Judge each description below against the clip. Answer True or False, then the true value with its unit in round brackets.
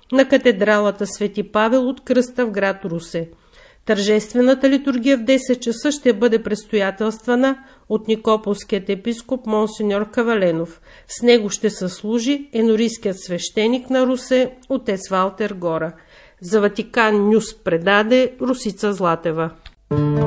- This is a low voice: False (220 Hz)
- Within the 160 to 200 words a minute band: False (120 wpm)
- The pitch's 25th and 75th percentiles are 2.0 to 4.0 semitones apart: True (3.7 semitones)